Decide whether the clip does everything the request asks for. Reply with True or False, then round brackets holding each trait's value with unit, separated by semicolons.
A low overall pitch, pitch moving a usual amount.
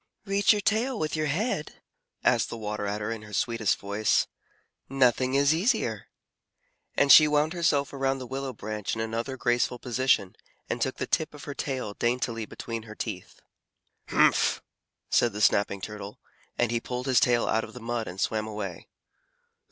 True (120 Hz; 4.6 semitones)